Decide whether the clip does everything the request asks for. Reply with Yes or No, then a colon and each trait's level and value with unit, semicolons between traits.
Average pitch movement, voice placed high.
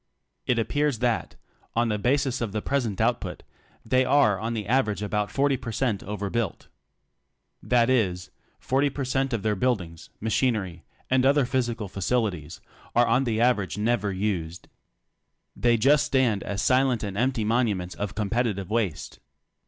No: average, 3.9 semitones; low, 115 Hz